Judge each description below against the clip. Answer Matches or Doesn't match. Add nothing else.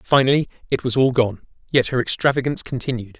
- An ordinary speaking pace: Matches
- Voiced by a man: Matches